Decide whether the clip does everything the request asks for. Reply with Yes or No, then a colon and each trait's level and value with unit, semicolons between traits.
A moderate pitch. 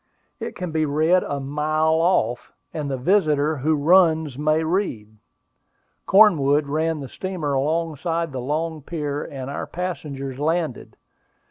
Yes: medium, 155 Hz